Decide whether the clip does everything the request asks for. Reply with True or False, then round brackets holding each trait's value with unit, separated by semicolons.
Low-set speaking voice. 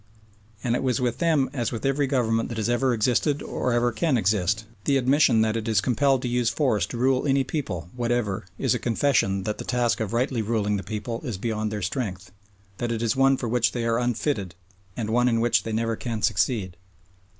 True (115 Hz)